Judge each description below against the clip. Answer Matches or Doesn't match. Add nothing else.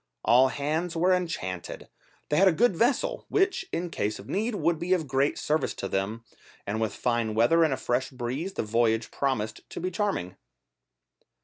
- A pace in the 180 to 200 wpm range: Matches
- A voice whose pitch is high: Doesn't match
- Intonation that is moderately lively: Doesn't match